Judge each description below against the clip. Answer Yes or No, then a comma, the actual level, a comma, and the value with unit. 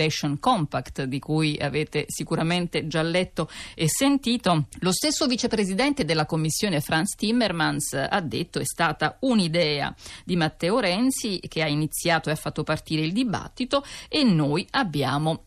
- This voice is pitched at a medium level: Yes, medium, 165 Hz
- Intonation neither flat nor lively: No, wide, 6.2 semitones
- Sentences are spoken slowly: No, average, 140 wpm